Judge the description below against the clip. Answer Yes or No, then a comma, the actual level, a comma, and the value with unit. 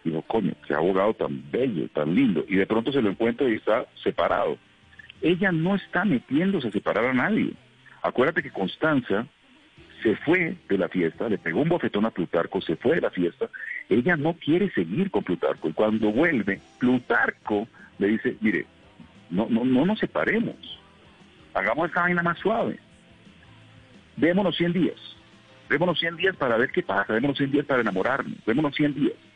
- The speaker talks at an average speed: Yes, average, 175 wpm